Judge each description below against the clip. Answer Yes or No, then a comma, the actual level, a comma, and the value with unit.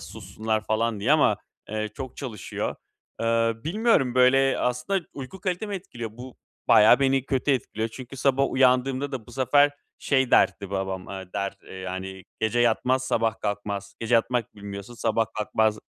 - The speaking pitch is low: Yes, low, 120 Hz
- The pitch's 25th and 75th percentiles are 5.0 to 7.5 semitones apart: No, average, 3.8 semitones